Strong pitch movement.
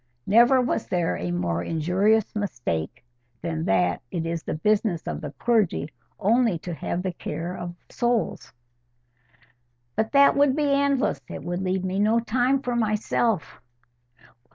Yes: wide, 6.3 semitones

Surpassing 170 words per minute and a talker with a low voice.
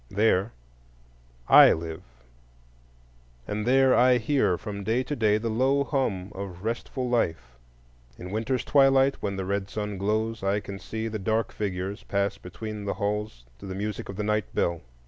No: average, 165 wpm; low, 105 Hz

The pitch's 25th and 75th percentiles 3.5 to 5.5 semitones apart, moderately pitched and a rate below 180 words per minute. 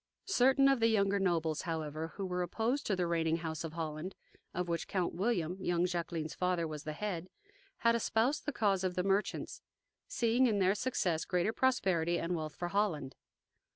No: average, 4.2 semitones; medium, 180 Hz; average, 185 wpm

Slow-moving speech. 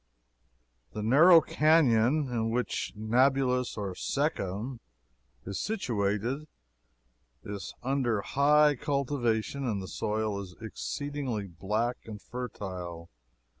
Yes: slow, 95 wpm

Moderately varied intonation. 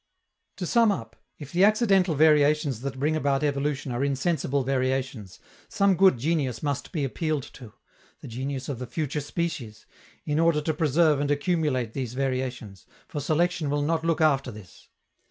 Yes: average, 3.5 semitones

